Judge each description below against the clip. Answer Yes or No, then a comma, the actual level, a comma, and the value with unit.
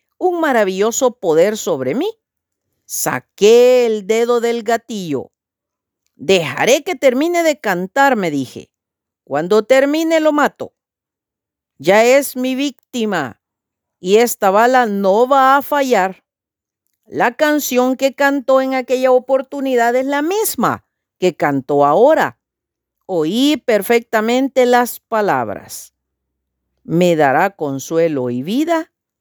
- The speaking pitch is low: No, high, 240 Hz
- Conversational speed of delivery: No, slow, 110 wpm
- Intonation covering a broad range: Yes, wide, 7.0 semitones